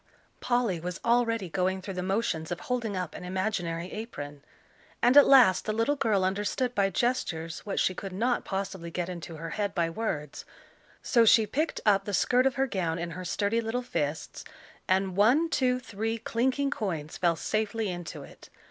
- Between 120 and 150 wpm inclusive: No, average, 185 wpm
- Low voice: No, high, 200 Hz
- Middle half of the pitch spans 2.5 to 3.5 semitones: No, average, 4.8 semitones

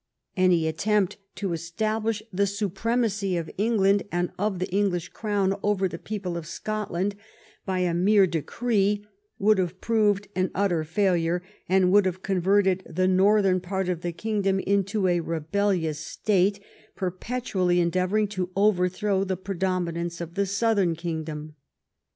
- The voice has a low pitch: No, high, 190 Hz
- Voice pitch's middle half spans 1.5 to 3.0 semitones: Yes, narrow, 2.6 semitones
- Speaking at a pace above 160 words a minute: No, average, 150 wpm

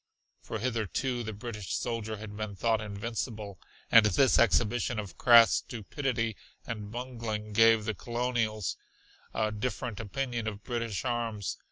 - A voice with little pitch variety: Yes, narrow, 2.1 semitones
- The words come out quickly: No, slow, 135 wpm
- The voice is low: Yes, low, 115 Hz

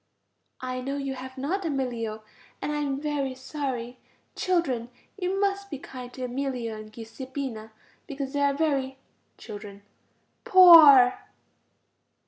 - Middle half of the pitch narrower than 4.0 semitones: Yes, average, 3.0 semitones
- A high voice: Yes, very high, 270 Hz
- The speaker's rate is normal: No, slow, 125 wpm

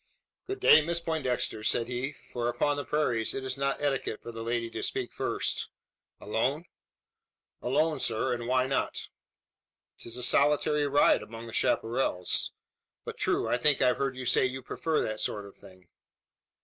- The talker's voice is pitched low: Yes, low, 130 Hz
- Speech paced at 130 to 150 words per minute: No, average, 170 wpm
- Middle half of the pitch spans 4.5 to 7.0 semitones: No, average, 3.6 semitones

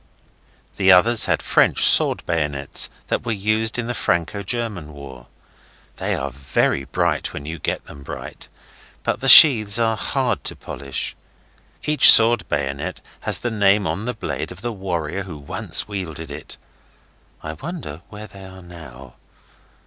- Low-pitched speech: Yes, very low, 95 Hz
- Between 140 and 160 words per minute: Yes, average, 155 wpm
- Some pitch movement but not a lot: No, wide, 7.2 semitones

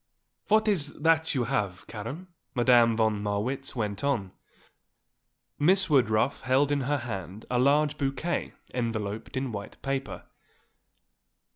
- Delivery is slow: Yes, slow, 125 wpm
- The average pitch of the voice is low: Yes, low, 130 Hz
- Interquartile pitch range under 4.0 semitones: No, average, 4.8 semitones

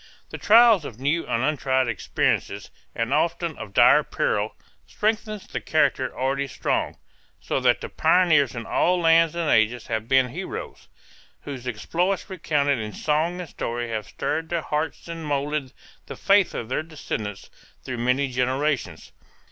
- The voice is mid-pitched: Yes, medium, 145 Hz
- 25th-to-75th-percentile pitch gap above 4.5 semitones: Yes, average, 5.0 semitones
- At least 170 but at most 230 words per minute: No, average, 155 wpm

